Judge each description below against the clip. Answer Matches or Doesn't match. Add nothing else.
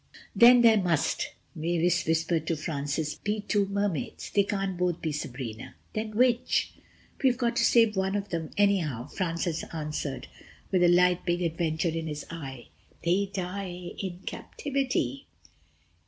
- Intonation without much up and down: Doesn't match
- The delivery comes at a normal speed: Matches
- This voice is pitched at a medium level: Matches